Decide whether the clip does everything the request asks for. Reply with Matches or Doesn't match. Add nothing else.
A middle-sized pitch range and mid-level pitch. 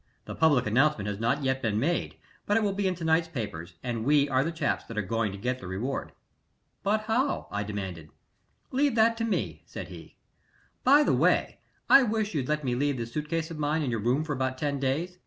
Doesn't match